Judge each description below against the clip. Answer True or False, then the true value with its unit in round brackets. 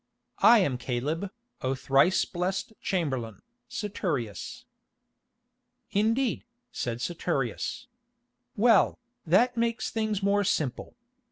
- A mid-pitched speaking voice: True (180 Hz)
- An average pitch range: False (8.4 semitones)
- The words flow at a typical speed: False (90 wpm)